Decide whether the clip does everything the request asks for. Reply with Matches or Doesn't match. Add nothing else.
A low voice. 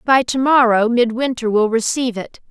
Doesn't match